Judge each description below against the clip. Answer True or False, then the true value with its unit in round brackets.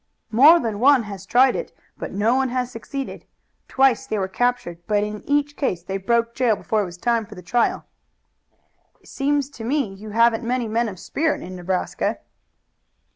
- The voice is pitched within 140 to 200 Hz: False (230 Hz)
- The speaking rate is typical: True (185 wpm)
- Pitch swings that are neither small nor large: True (4.0 semitones)